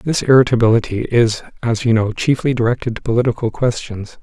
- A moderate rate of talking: Yes, average, 155 wpm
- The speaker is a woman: No, male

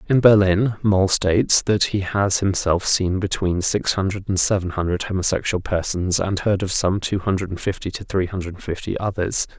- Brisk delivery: No, average, 180 wpm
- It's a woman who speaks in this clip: No, male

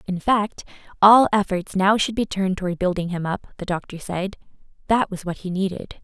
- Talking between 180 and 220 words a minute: Yes, average, 200 wpm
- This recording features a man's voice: No, female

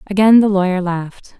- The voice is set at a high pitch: Yes, high, 195 Hz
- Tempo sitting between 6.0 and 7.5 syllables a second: No, 5.5 syllables/s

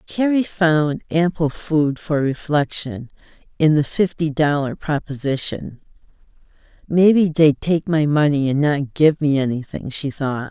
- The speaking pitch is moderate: Yes, medium, 150 Hz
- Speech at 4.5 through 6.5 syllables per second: No, 4.2 syllables/s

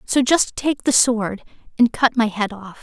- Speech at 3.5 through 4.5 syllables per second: Yes, 4.2 syllables/s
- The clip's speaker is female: Yes, female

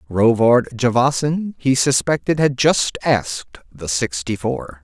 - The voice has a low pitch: Yes, low, 120 Hz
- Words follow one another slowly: Yes, slow, 110 wpm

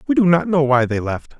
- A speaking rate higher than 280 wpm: Yes, fast, 300 wpm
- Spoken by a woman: No, male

